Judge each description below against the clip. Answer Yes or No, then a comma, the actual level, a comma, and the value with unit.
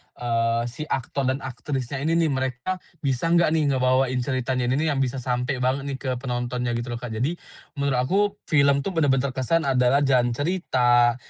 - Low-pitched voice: Yes, low, 130 Hz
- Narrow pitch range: Yes, narrow, 2.3 semitones